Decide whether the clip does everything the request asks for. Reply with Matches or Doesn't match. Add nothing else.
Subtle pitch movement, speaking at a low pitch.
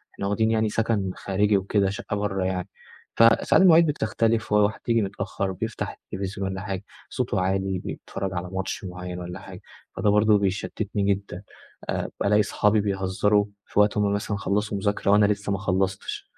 Matches